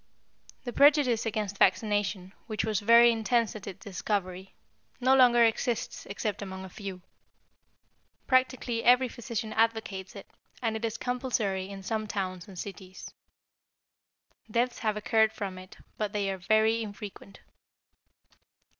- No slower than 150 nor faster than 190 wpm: No, slow, 135 wpm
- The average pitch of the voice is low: No, high, 215 Hz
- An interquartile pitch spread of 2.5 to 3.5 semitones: Yes, average, 3.1 semitones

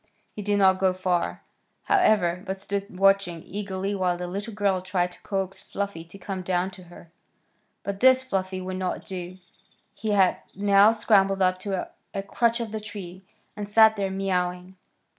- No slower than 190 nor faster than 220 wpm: No, average, 175 wpm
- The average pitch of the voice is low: No, high, 195 Hz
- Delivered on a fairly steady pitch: Yes, narrow, 1.7 semitones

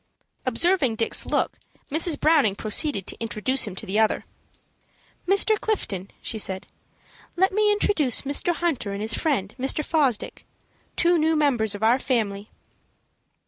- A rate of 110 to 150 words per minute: Yes, average, 140 wpm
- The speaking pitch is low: No, very high, 260 Hz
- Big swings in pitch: Yes, wide, 7.1 semitones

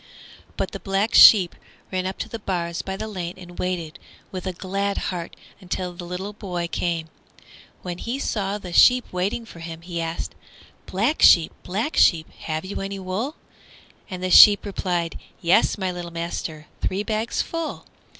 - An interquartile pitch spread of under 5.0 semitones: Yes, average, 2.7 semitones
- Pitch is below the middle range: No, medium, 185 Hz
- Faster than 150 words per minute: Yes, average, 170 wpm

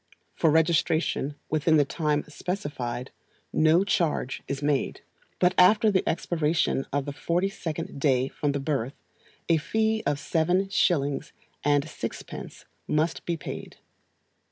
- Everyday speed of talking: No, slow, 130 wpm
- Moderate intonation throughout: Yes, average, 3.4 semitones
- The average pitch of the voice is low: No, medium, 155 Hz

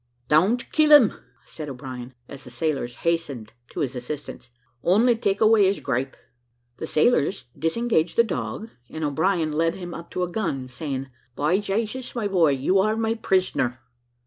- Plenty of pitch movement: Yes, wide, 7.0 semitones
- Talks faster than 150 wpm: Yes, average, 165 wpm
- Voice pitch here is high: No, medium, 165 Hz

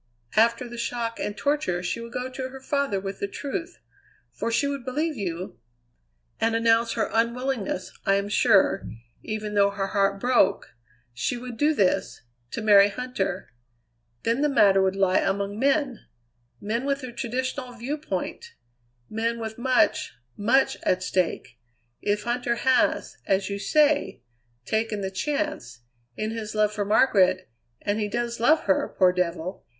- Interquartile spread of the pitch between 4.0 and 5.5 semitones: Yes, average, 4.3 semitones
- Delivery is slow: No, average, 155 wpm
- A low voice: No, high, 225 Hz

